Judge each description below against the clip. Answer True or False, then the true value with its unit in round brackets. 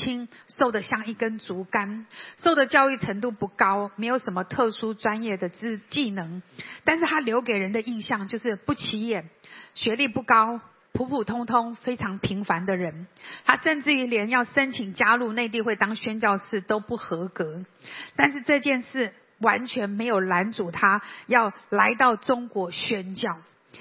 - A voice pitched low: False (225 Hz)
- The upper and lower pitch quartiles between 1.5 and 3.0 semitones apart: False (3.5 semitones)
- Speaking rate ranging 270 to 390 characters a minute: False (240 characters per minute)